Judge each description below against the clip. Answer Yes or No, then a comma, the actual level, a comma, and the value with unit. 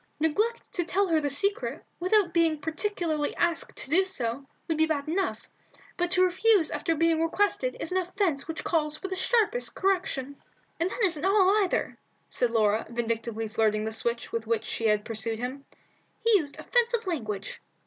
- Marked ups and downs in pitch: Yes, wide, 7.5 semitones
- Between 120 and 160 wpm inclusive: No, average, 180 wpm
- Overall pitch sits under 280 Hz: No, very high, 325 Hz